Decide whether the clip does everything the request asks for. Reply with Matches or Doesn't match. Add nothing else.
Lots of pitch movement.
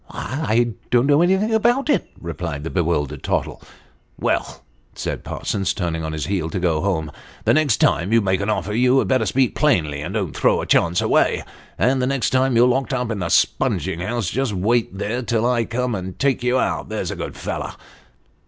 Matches